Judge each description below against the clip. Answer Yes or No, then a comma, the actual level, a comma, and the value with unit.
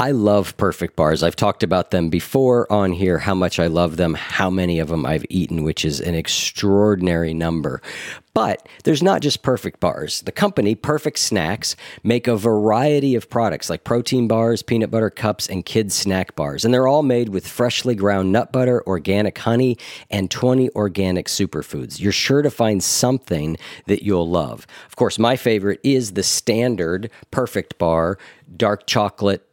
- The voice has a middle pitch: No, low, 100 Hz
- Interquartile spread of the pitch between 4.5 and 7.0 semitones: Yes, average, 5.2 semitones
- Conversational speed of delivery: Yes, average, 175 wpm